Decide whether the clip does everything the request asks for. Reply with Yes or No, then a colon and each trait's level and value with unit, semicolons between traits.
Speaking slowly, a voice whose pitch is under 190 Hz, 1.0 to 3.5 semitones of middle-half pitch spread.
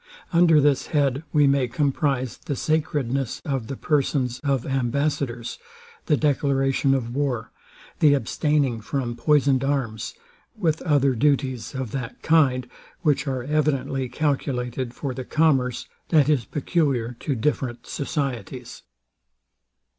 Yes: slow, 125 wpm; low, 135 Hz; average, 2.7 semitones